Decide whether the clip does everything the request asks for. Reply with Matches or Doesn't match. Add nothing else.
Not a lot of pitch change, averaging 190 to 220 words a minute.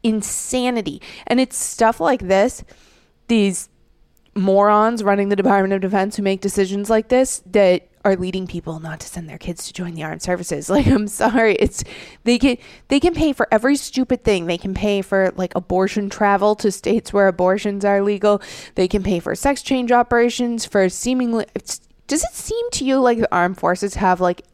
Doesn't match